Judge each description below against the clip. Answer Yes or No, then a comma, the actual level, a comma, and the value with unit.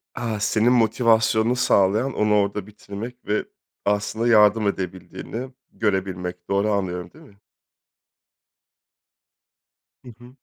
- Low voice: Yes, low, 105 Hz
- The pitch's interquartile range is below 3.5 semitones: Yes, average, 2.8 semitones